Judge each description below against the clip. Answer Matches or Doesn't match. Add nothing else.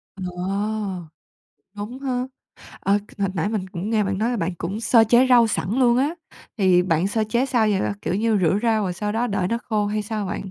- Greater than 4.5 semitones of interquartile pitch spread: Doesn't match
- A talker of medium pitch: Doesn't match